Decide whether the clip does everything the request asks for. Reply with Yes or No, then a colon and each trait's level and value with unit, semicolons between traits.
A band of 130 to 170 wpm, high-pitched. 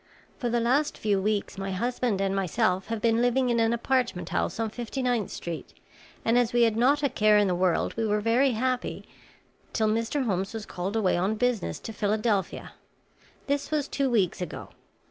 No: average, 195 wpm; high, 225 Hz